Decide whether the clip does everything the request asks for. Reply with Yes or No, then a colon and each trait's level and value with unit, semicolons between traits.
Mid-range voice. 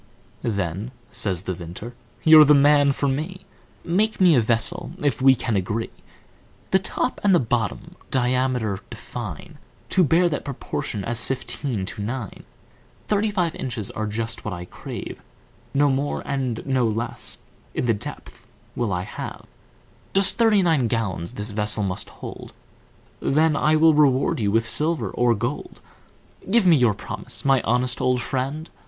No: low, 125 Hz